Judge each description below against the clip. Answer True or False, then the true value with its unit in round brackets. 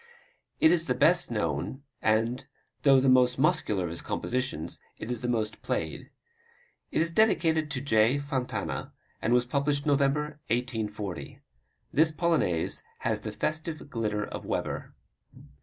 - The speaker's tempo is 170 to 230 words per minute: False (140 wpm)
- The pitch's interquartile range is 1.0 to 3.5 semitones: False (5.4 semitones)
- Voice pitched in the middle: False (125 Hz)